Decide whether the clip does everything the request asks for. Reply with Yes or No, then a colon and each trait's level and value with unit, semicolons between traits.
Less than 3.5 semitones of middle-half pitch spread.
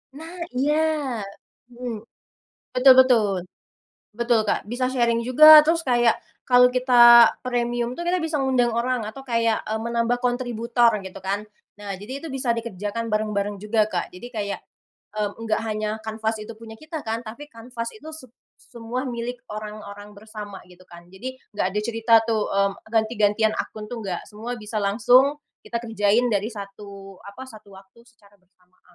Yes: average, 2.8 semitones